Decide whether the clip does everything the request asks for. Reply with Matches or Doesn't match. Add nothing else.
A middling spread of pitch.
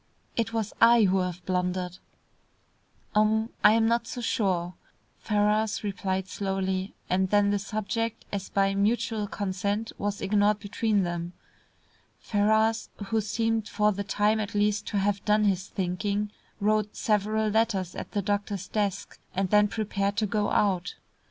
Doesn't match